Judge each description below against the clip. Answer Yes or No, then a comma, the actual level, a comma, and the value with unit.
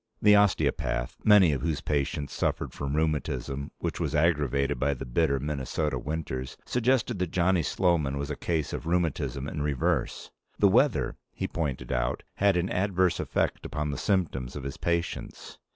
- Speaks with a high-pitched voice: No, very low, 75 Hz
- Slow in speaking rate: No, average, 165 wpm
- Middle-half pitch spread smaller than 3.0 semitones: No, average, 3.9 semitones